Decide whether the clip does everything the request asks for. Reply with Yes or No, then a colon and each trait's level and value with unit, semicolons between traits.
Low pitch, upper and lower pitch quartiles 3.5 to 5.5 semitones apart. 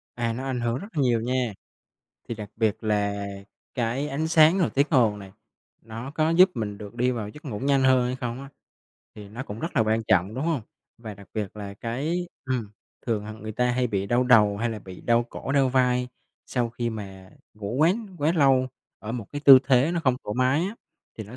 Yes: low, 120 Hz; average, 3.9 semitones